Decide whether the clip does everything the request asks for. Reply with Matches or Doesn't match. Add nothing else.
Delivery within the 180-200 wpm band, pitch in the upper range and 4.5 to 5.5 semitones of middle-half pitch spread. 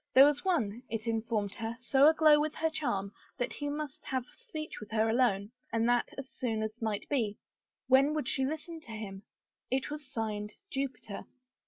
Matches